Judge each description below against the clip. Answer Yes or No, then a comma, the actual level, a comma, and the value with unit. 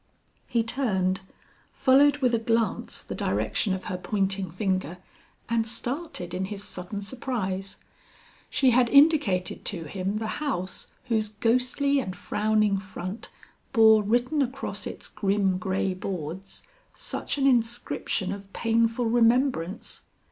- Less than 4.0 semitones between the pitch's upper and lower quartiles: No, average, 4.3 semitones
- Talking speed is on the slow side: Yes, slow, 125 wpm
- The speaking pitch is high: Yes, high, 215 Hz